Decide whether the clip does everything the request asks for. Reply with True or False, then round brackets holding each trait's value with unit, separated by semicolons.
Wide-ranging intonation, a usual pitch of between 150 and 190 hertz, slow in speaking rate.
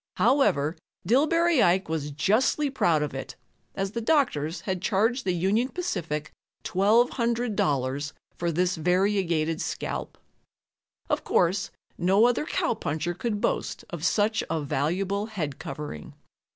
True (6.2 semitones; 185 Hz; 125 wpm)